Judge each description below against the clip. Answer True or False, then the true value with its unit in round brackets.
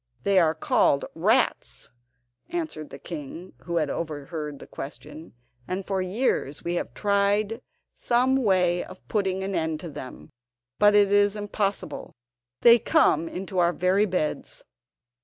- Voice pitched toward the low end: False (185 Hz)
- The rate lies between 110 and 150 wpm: True (140 wpm)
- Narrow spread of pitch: False (4.5 semitones)